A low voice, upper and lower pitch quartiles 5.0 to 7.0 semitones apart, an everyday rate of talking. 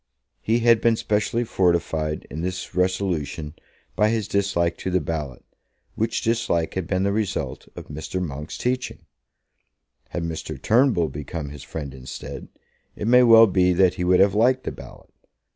Yes: very low, 95 Hz; average, 5.3 semitones; average, 160 wpm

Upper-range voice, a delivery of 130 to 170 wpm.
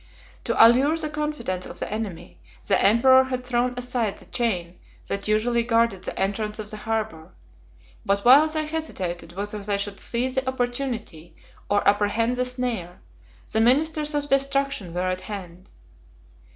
Yes: high, 230 Hz; average, 155 wpm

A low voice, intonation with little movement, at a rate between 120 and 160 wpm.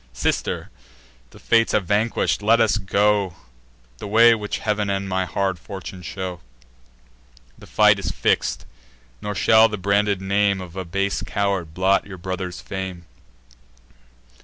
Yes: low, 100 Hz; narrow, 1.8 semitones; average, 140 wpm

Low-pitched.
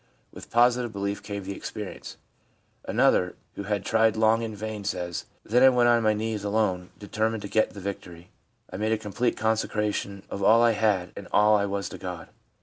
Yes: low, 105 Hz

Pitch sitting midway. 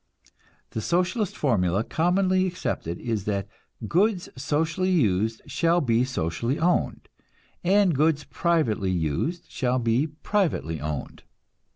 Yes: medium, 145 Hz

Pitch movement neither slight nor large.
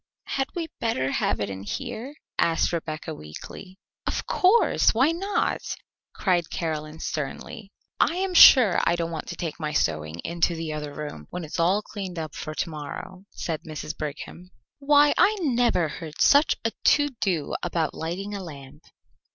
No: wide, 6.8 semitones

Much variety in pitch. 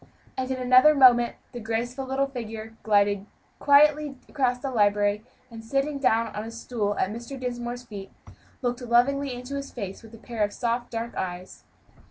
No: average, 3.0 semitones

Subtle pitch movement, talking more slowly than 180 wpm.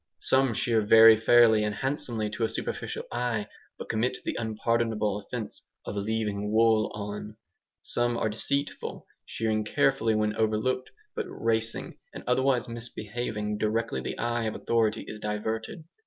Yes: narrow, 1.8 semitones; average, 140 wpm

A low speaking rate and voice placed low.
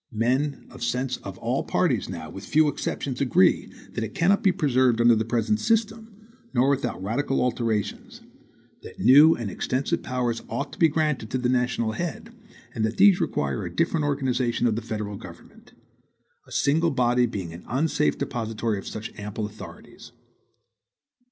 No: average, 165 wpm; low, 125 Hz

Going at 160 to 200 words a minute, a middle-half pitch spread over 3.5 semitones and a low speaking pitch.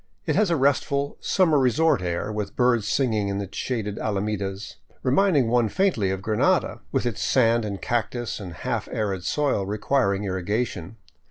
Yes: average, 165 wpm; average, 5.0 semitones; low, 110 Hz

